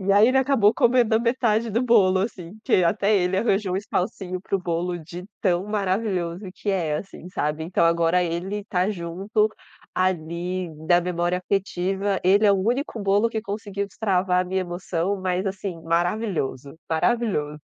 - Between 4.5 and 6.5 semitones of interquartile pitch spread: No, average, 3.0 semitones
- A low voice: No, high, 190 Hz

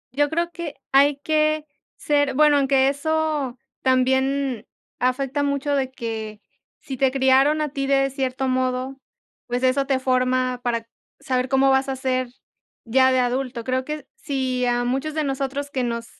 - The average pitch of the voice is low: No, very high, 265 Hz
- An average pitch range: No, narrow, 1.8 semitones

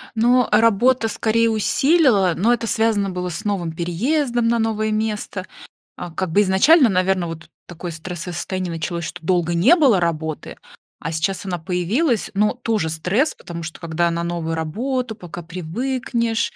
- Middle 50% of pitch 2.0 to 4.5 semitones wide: No, average, 5.1 semitones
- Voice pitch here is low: No, high, 190 Hz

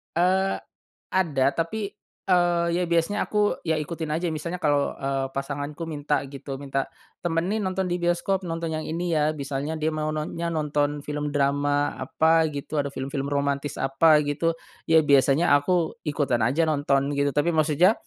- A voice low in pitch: No, medium, 155 Hz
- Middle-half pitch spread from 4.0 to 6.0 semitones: No, average, 3.0 semitones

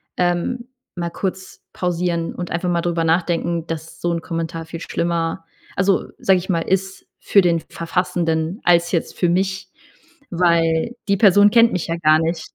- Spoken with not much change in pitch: Yes, narrow, 2.0 semitones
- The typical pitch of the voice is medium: Yes, medium, 170 Hz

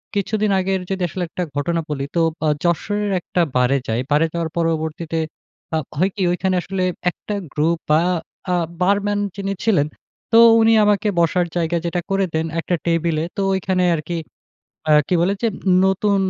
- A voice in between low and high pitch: Yes, medium, 175 Hz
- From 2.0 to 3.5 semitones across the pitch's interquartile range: Yes, average, 3.2 semitones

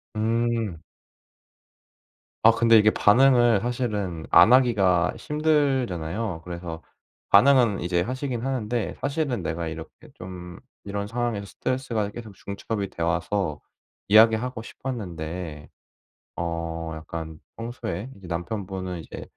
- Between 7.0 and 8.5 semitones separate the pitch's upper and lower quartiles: No, wide, 5.5 semitones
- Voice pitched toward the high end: No, low, 105 Hz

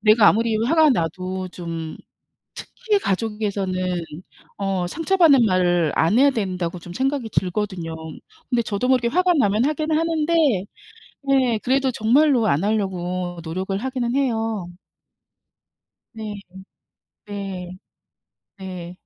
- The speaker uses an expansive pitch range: Yes, wide, 6.2 semitones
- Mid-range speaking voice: No, high, 210 Hz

